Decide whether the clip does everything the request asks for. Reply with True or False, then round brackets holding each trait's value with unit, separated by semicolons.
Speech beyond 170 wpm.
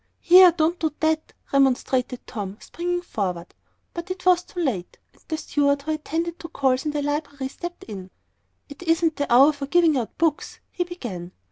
True (180 wpm)